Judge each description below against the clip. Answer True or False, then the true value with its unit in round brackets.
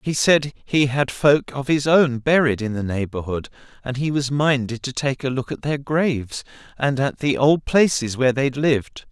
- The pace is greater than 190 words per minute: True (205 wpm)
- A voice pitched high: False (135 Hz)